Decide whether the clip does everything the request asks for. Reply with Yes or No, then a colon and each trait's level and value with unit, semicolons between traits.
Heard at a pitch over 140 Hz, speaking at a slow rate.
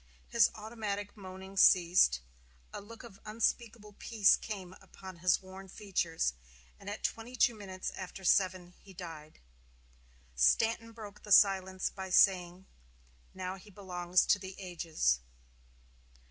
Yes: high, 190 Hz; slow, 130 wpm